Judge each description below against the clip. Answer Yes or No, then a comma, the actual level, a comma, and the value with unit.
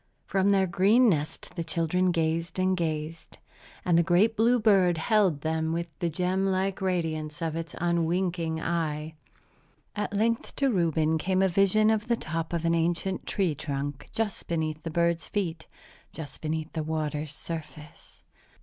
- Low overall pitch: No, medium, 170 Hz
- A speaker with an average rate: Yes, average, 160 wpm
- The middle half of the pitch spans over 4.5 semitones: No, average, 3.1 semitones